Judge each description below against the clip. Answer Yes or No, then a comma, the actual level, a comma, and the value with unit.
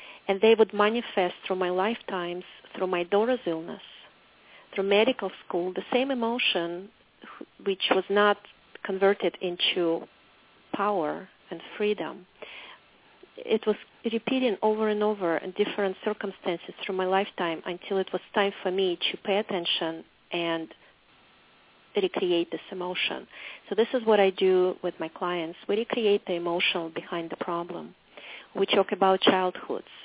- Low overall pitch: No, high, 195 Hz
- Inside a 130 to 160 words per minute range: Yes, average, 140 wpm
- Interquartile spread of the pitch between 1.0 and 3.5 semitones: Yes, average, 2.9 semitones